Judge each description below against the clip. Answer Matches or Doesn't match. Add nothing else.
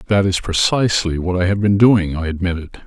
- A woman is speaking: Doesn't match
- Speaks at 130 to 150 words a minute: Doesn't match